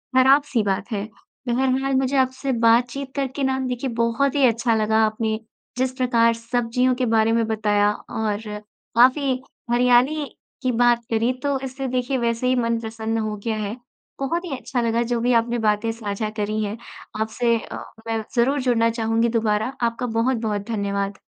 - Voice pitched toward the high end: Yes, high, 235 Hz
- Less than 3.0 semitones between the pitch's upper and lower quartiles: Yes, narrow, 2.6 semitones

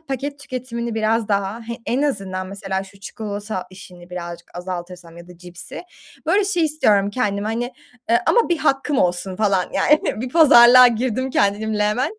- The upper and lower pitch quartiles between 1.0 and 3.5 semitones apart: No, average, 5.2 semitones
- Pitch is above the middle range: Yes, high, 215 Hz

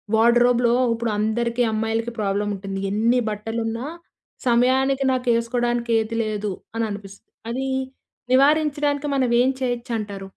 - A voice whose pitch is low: No, high, 235 Hz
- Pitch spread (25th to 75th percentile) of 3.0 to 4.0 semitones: No, narrow, 2.5 semitones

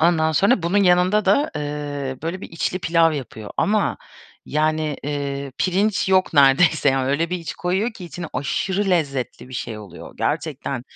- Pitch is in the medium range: Yes, medium, 160 Hz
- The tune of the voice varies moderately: Yes, average, 4.6 semitones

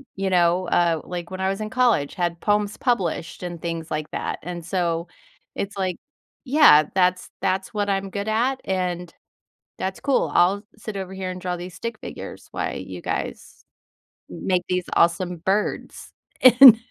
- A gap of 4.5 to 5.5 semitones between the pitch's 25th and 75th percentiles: No, average, 2.7 semitones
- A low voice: No, medium, 185 Hz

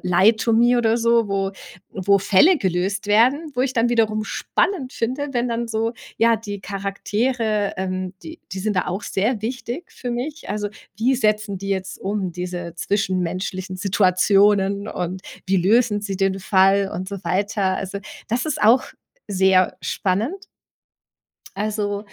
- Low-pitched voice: No, high, 205 Hz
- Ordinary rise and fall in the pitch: Yes, average, 3.4 semitones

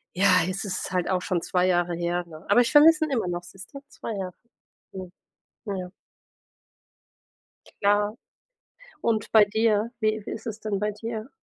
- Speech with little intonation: No, average, 3.3 semitones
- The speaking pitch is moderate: No, high, 205 Hz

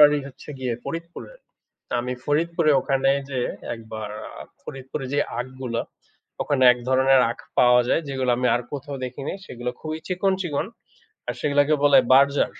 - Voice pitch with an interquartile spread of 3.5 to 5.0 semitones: No, average, 2.7 semitones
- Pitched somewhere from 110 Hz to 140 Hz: Yes, low, 135 Hz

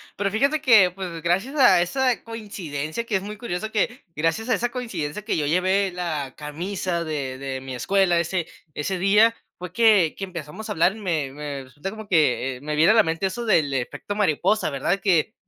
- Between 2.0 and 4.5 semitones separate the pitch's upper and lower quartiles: No, wide, 5.6 semitones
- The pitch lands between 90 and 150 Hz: No, medium, 180 Hz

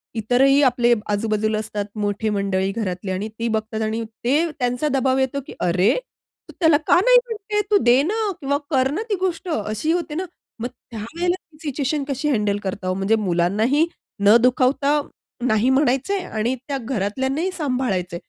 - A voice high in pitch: Yes, high, 245 Hz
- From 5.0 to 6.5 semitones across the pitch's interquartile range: Yes, wide, 5.5 semitones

